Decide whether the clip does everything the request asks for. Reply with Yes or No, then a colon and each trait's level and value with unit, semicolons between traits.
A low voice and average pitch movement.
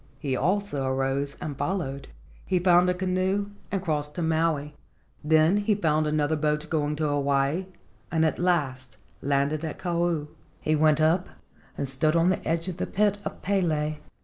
No: medium, 155 Hz; average, 3.4 semitones